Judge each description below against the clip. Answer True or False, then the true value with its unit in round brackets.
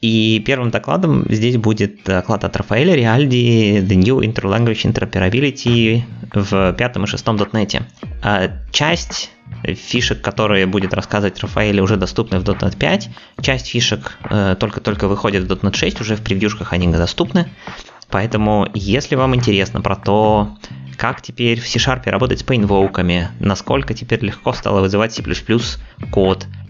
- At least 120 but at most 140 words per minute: True (135 wpm)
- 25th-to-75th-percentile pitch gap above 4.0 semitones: False (3.2 semitones)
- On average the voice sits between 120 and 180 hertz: False (105 Hz)